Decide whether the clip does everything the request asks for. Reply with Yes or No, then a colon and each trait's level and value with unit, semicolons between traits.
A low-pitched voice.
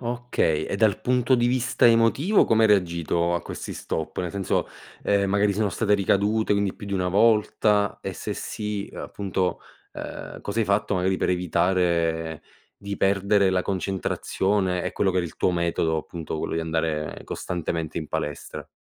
Yes: very low, 95 Hz